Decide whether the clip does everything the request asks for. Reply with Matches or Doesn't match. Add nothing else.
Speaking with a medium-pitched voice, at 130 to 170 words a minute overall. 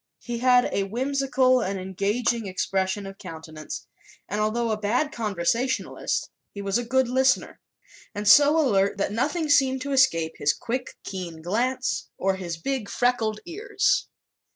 Doesn't match